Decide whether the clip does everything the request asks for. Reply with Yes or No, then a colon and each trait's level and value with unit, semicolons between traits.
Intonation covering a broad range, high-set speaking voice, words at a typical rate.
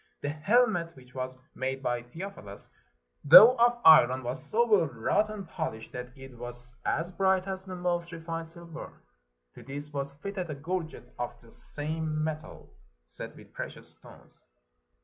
No: wide, 5.9 semitones; medium, 155 Hz; average, 160 wpm